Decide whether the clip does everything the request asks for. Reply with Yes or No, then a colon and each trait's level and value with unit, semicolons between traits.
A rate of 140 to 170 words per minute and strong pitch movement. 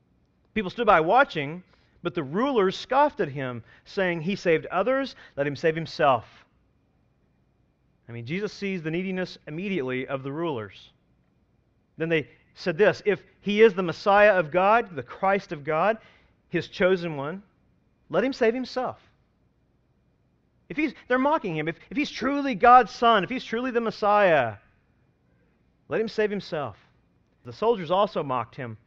Yes: average, 155 wpm; wide, 6.4 semitones